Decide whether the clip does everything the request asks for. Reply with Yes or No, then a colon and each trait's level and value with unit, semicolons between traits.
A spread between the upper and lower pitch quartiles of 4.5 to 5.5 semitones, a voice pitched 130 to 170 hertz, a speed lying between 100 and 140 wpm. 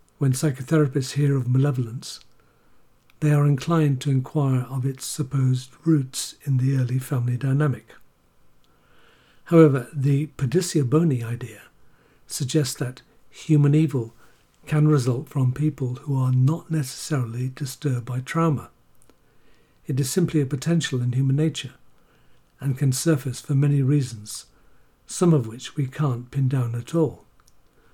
No: average, 2.7 semitones; medium, 140 Hz; slow, 135 wpm